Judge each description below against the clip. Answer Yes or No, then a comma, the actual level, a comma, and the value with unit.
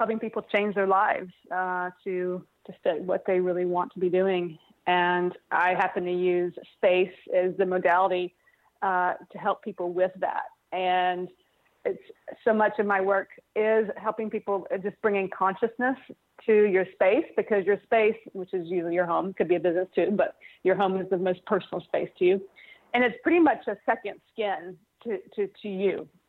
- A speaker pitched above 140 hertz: Yes, high, 190 Hz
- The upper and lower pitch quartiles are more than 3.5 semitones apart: No, average, 2.9 semitones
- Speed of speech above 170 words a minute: Yes, average, 185 wpm